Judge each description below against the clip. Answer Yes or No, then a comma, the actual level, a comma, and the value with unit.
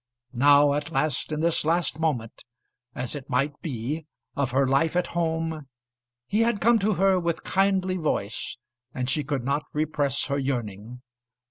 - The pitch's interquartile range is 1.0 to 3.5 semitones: No, average, 4.0 semitones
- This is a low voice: No, medium, 150 Hz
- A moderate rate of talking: Yes, average, 160 wpm